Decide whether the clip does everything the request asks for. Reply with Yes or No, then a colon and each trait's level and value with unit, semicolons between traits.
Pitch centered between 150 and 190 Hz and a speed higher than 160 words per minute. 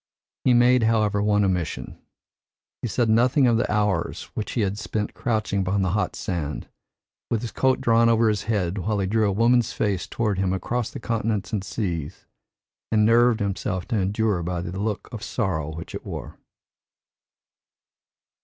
No: low, 105 Hz; average, 170 wpm